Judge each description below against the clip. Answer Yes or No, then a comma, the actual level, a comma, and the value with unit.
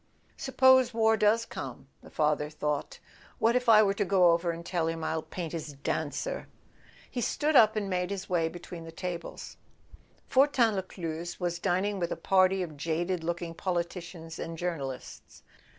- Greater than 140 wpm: Yes, average, 165 wpm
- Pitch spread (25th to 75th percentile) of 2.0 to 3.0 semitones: No, average, 3.8 semitones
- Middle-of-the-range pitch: Yes, medium, 175 Hz